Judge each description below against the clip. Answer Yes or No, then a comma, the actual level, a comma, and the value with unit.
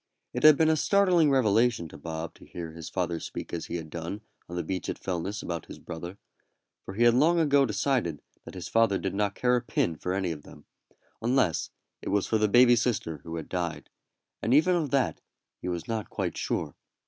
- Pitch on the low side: Yes, low, 100 Hz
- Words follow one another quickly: Yes, fast, 220 wpm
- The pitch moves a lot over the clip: Yes, wide, 6.7 semitones